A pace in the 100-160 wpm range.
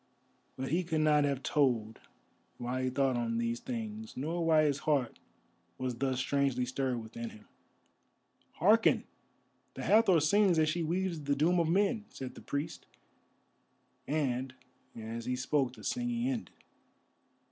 Yes: average, 145 wpm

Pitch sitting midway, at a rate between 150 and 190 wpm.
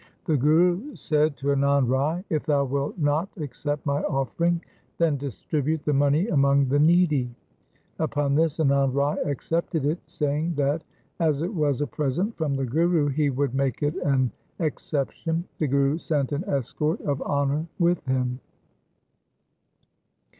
Yes: medium, 145 Hz; average, 155 wpm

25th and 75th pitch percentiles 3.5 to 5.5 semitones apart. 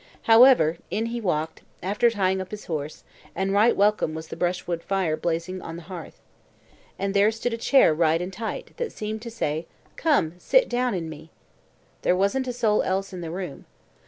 Yes: average, 5.1 semitones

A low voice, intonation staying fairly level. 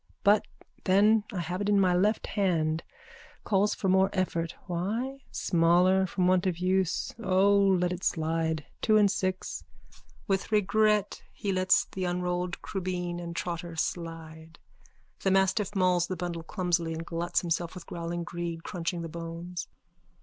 No: medium, 180 Hz; narrow, 2.3 semitones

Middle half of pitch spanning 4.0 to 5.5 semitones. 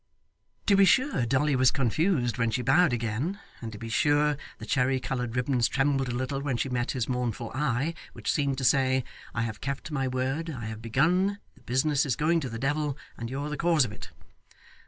No: average, 3.5 semitones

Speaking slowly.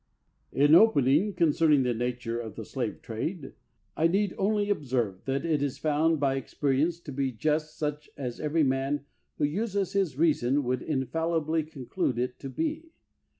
No: average, 160 wpm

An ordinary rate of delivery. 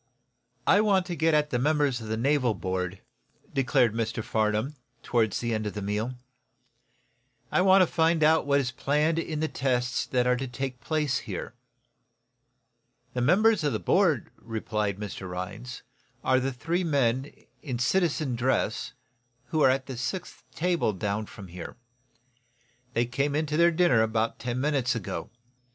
Yes: average, 165 wpm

